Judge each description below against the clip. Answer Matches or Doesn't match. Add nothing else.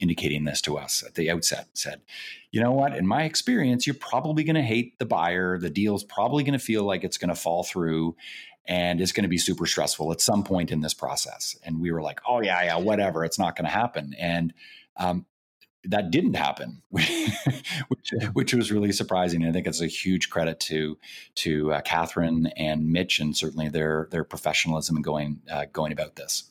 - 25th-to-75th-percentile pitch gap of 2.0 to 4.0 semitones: Doesn't match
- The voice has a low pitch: Matches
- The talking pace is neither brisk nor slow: Doesn't match